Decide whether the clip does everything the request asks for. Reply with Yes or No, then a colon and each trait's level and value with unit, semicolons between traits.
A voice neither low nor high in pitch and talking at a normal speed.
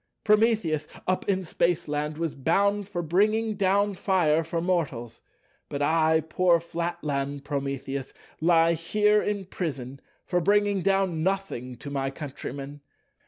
No: medium, 165 Hz; slow, 120 wpm